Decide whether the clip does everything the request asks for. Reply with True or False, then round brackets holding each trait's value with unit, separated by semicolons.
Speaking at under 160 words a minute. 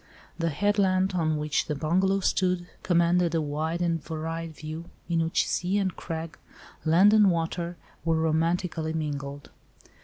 True (145 wpm)